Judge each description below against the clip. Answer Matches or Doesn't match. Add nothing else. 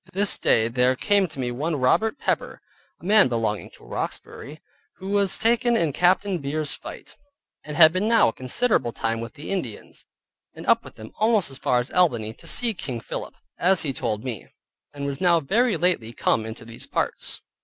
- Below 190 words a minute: Doesn't match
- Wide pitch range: Matches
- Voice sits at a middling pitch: Matches